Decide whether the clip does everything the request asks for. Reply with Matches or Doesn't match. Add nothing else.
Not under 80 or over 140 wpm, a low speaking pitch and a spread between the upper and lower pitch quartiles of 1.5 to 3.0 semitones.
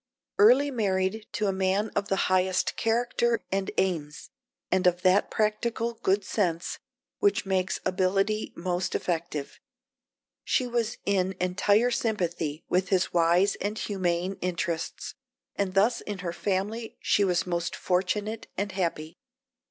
Doesn't match